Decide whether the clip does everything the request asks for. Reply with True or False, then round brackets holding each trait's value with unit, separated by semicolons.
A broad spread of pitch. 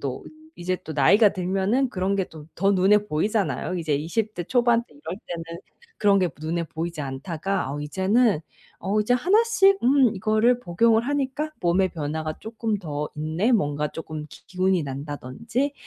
True (6.3 semitones)